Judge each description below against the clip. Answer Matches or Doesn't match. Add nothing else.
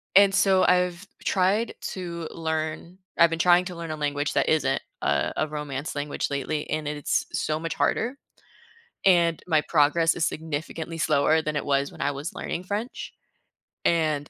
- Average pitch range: Matches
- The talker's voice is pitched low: Doesn't match